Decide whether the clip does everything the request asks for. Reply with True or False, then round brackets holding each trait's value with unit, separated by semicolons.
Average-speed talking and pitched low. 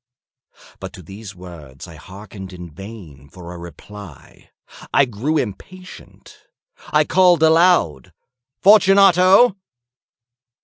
False (100 wpm; 100 Hz)